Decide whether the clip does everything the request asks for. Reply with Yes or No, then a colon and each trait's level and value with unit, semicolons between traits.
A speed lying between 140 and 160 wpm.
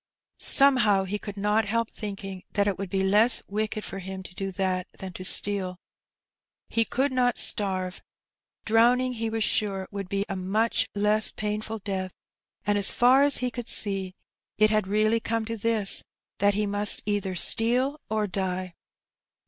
No: average, 170 wpm